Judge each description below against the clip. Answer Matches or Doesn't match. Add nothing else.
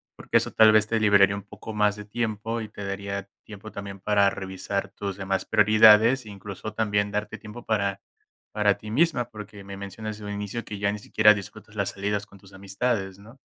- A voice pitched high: Doesn't match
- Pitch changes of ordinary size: Doesn't match